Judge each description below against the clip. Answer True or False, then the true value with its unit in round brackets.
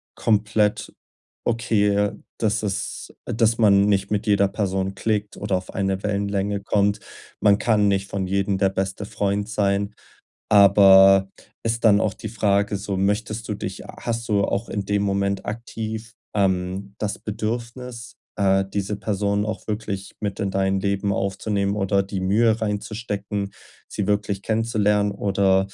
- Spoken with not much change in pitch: True (1.5 semitones)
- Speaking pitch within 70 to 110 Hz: True (100 Hz)